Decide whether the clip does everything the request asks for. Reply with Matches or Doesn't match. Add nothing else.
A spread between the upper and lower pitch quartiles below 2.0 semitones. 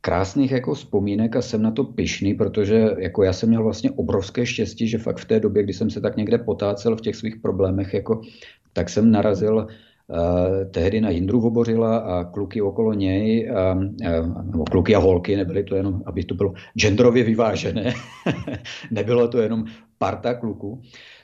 Doesn't match